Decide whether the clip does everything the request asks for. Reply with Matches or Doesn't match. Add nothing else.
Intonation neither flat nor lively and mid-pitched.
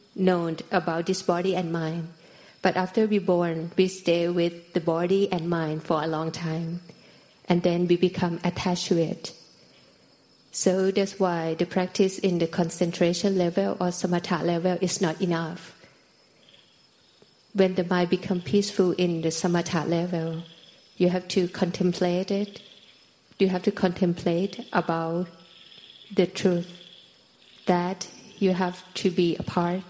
Doesn't match